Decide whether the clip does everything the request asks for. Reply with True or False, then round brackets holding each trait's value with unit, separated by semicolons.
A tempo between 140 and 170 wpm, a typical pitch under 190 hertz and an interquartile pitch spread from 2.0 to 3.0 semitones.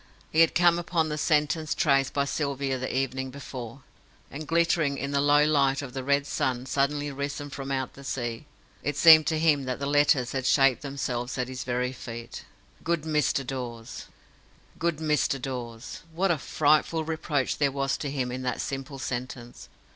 False (180 wpm; 140 Hz; 2.6 semitones)